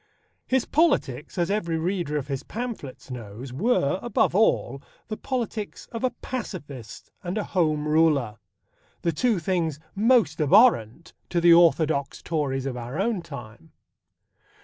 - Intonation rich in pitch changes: Yes, wide, 7.3 semitones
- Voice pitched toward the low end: No, medium, 165 Hz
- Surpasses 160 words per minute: No, average, 140 wpm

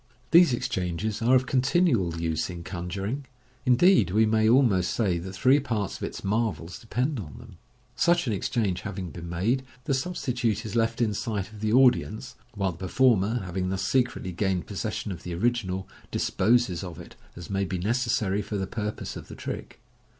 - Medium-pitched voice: No, low, 105 Hz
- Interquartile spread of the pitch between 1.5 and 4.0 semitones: No, average, 4.7 semitones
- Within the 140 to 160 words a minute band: No, average, 185 wpm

